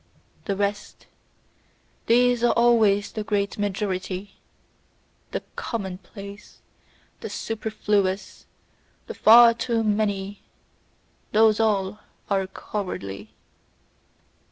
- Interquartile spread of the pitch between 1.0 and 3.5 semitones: Yes, narrow, 2.4 semitones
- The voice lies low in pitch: No, high, 205 Hz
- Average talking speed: No, slow, 85 wpm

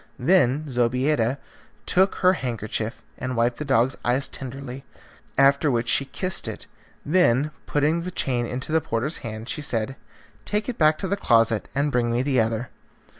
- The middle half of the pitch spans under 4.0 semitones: No, average, 4.4 semitones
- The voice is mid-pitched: No, low, 130 Hz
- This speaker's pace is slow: No, average, 170 wpm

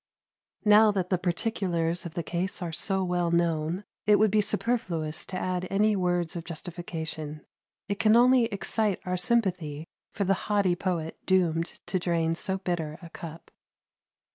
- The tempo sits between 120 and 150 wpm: No, average, 160 wpm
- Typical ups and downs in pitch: Yes, average, 3.2 semitones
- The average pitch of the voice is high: No, medium, 180 Hz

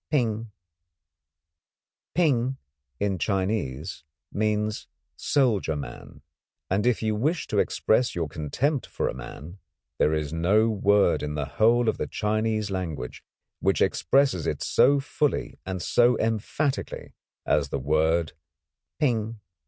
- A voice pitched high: No, low, 105 Hz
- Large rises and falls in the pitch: Yes, wide, 6.7 semitones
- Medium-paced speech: No, slow, 120 wpm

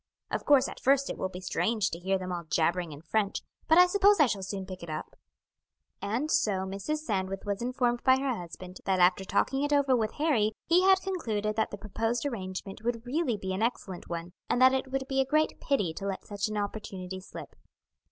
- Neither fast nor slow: No, fast, 220 wpm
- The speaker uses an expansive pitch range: Yes, wide, 6.0 semitones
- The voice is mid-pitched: No, high, 215 Hz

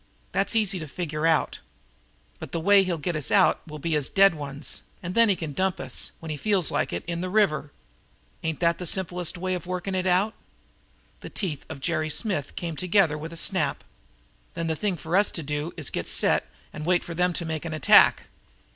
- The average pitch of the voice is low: No, medium, 170 Hz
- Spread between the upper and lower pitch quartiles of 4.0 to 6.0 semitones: No, average, 3.2 semitones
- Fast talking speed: Yes, fast, 220 wpm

